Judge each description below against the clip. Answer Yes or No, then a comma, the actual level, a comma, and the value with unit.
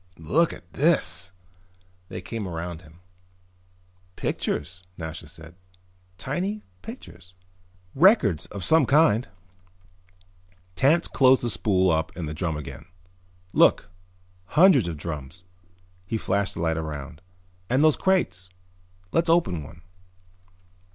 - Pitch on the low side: Yes, very low, 90 Hz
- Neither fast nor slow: No, slow, 115 wpm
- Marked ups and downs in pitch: Yes, wide, 9.0 semitones